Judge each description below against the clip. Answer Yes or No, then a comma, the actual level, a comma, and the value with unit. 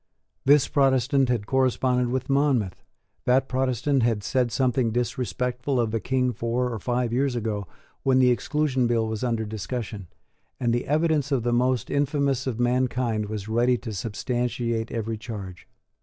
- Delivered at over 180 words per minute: No, average, 155 wpm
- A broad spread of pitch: No, narrow, 2.4 semitones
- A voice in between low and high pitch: No, low, 125 Hz